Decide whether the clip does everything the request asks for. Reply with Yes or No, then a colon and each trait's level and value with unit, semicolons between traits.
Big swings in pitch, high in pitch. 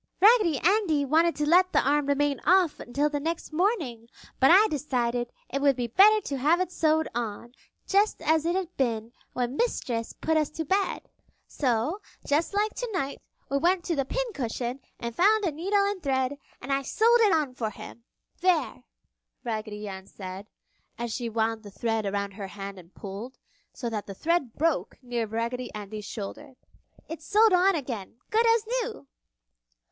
Yes: wide, 7.4 semitones; very high, 280 Hz